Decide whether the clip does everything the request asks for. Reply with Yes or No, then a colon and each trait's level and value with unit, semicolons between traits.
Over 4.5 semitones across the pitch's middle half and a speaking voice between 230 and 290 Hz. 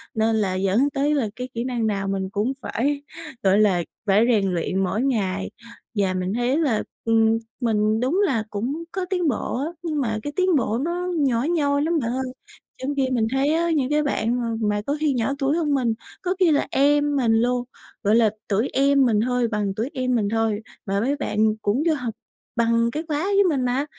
Yes: average, 4.9 semitones; high, 245 Hz